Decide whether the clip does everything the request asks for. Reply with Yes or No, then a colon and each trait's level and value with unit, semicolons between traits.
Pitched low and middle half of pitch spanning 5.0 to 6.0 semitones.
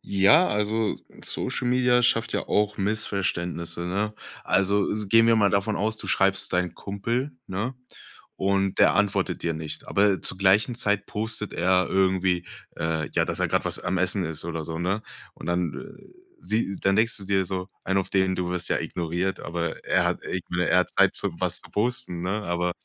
No: very low, 95 Hz; average, 2.8 semitones